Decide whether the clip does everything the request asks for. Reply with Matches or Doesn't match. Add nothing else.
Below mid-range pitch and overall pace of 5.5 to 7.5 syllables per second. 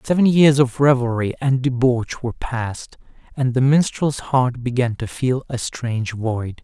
Doesn't match